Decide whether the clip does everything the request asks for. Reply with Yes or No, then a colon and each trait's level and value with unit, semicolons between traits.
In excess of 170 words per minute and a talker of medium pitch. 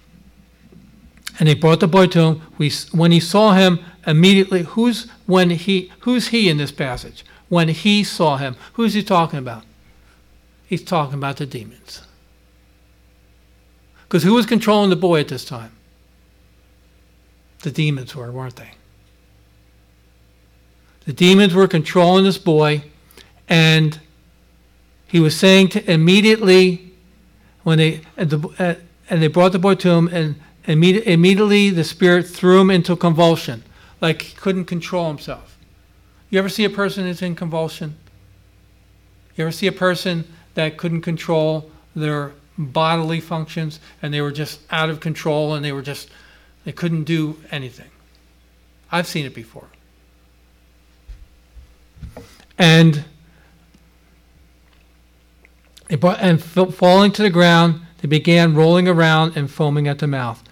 No: slow, 135 wpm; medium, 155 Hz